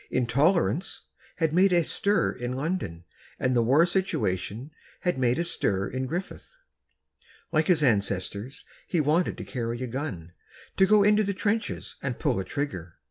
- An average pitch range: No, wide, 7.3 semitones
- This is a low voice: No, medium, 145 Hz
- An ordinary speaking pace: Yes, average, 155 wpm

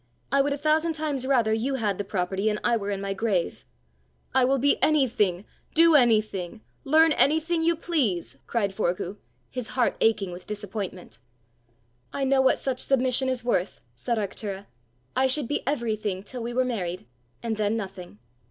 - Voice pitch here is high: Yes, high, 230 Hz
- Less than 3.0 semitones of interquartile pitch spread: No, average, 5.3 semitones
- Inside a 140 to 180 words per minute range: Yes, average, 170 wpm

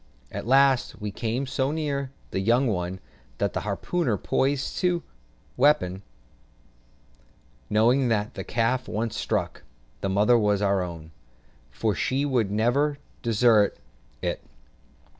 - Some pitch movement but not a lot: Yes, average, 4.7 semitones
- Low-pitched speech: Yes, low, 115 Hz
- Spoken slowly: Yes, slow, 125 wpm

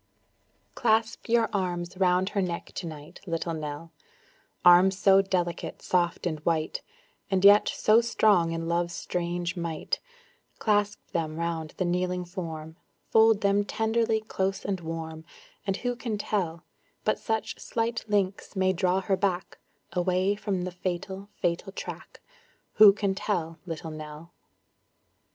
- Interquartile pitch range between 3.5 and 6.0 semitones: No, average, 3.1 semitones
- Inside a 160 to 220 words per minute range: No, average, 140 wpm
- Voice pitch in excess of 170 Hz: Yes, medium, 185 Hz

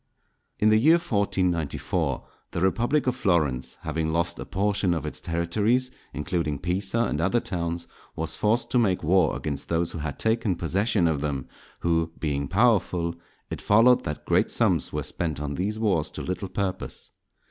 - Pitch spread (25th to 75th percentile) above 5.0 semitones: No, average, 4.7 semitones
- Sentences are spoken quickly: No, average, 170 wpm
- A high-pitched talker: No, very low, 90 Hz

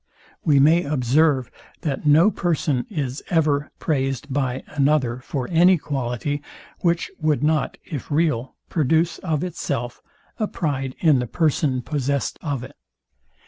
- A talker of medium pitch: Yes, medium, 145 Hz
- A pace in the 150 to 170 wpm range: No, slow, 135 wpm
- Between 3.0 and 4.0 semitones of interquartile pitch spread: Yes, average, 3.3 semitones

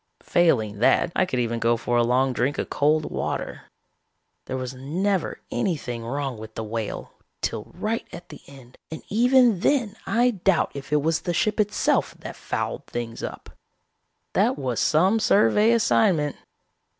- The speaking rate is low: No, average, 160 wpm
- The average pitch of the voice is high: No, medium, 150 Hz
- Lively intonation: Yes, wide, 8.4 semitones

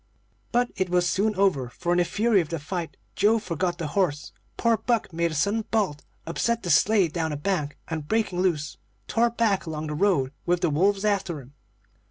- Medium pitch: Yes, medium, 180 Hz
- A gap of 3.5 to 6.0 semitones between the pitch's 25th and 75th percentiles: Yes, average, 4.6 semitones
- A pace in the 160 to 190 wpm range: No, fast, 205 wpm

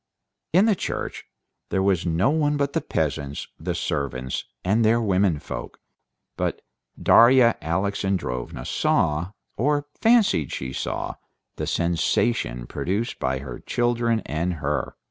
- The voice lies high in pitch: No, very low, 95 Hz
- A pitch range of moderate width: No, wide, 8.1 semitones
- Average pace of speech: No, slow, 125 wpm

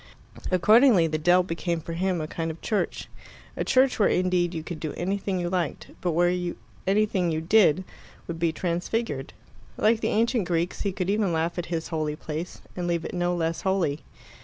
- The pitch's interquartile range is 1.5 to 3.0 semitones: Yes, narrow, 2.5 semitones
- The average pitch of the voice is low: No, medium, 175 Hz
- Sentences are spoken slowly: No, average, 190 wpm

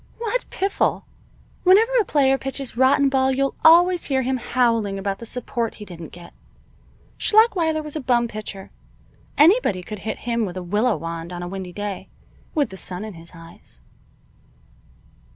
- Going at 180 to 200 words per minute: No, average, 165 wpm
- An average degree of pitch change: No, wide, 6.9 semitones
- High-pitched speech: Yes, high, 235 Hz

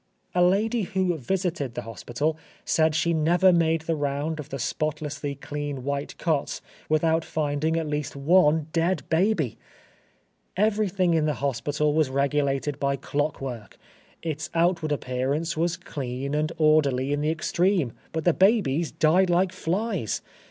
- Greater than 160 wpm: No, average, 145 wpm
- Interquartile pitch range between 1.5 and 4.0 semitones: Yes, average, 3.3 semitones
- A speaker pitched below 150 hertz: No, medium, 155 Hz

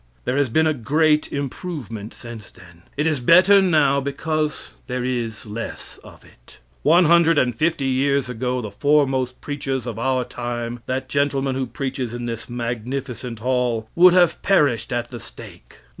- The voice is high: No, low, 130 Hz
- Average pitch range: Yes, average, 3.7 semitones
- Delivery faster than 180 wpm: No, average, 165 wpm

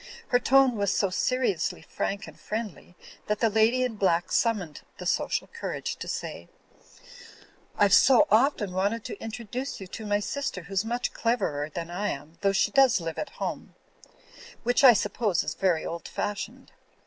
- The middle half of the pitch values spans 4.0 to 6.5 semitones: Yes, average, 4.6 semitones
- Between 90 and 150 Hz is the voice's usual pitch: No, high, 210 Hz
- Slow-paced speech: No, average, 170 wpm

